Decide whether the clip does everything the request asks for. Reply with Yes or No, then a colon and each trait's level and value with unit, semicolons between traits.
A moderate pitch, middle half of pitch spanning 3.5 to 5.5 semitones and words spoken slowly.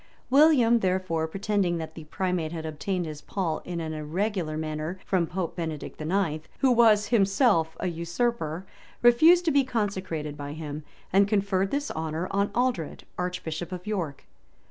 No: medium, 180 Hz; average, 4.5 semitones; average, 160 wpm